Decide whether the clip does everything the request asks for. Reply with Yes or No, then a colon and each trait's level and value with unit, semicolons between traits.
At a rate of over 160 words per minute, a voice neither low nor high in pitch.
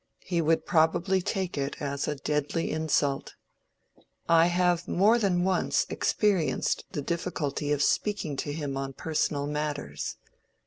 No: slow, 135 wpm; medium, 160 Hz